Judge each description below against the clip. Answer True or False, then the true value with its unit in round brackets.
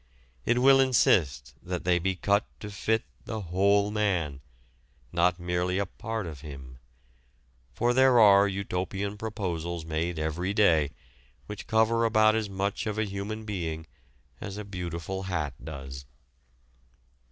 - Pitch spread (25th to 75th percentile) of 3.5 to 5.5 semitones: True (4.1 semitones)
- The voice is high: False (95 Hz)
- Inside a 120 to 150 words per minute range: True (140 wpm)